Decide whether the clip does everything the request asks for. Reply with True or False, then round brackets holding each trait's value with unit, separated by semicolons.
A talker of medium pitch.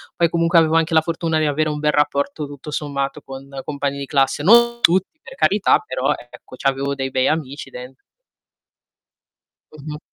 True (150 Hz)